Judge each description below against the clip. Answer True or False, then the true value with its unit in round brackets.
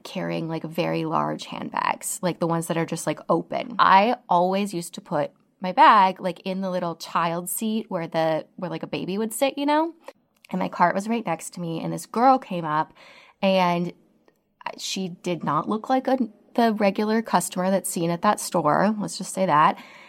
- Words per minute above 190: True (205 wpm)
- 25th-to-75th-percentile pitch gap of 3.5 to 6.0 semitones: True (4.4 semitones)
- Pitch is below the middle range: False (185 Hz)